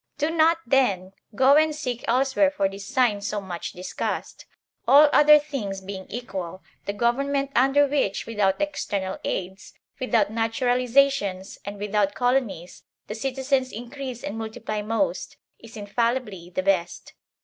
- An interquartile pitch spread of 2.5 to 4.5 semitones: No, wide, 5.5 semitones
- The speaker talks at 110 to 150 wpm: Yes, average, 140 wpm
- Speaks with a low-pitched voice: No, high, 230 Hz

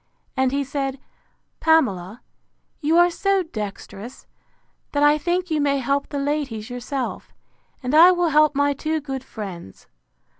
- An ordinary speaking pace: Yes, average, 145 wpm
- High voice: Yes, very high, 285 Hz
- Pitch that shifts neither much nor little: Yes, average, 3.8 semitones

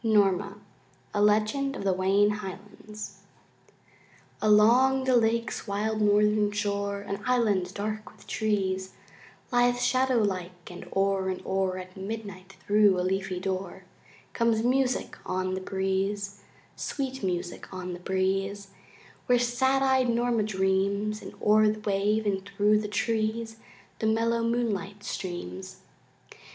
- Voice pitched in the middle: No, high, 205 Hz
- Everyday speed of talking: No, slow, 130 wpm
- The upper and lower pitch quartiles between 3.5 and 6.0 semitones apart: No, average, 2.7 semitones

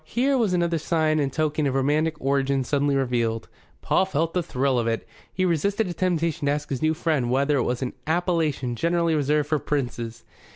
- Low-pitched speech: No, medium, 150 Hz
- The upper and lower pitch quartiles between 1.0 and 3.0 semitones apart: No, average, 3.7 semitones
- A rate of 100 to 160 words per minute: No, average, 200 wpm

